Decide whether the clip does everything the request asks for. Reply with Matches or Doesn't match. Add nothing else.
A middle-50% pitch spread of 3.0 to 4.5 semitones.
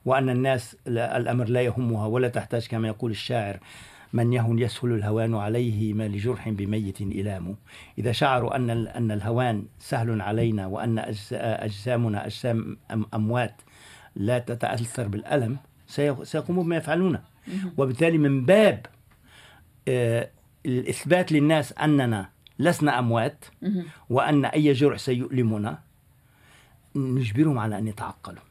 Matches